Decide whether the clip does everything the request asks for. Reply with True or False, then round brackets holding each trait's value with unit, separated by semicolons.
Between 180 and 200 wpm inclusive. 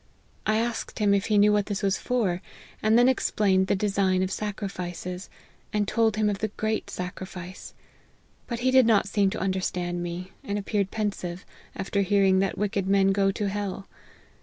True (185 wpm)